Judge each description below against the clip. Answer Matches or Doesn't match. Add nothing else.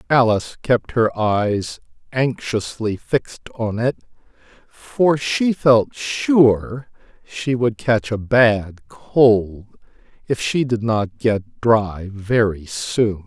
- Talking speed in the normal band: Doesn't match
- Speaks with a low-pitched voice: Matches